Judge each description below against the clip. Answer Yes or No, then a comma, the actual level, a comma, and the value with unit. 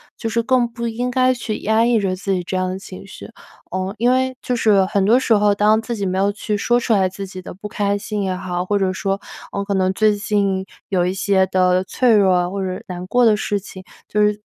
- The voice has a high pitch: Yes, high, 200 Hz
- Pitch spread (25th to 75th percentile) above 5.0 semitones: No, average, 2.9 semitones